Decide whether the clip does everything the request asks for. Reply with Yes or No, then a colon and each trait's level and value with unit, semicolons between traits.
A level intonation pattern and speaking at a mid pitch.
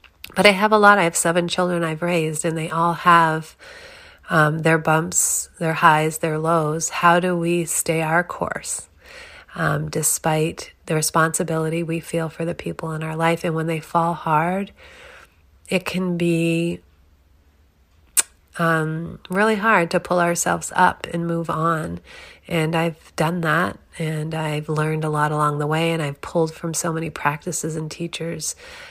Yes: narrow, 1.7 semitones; medium, 165 Hz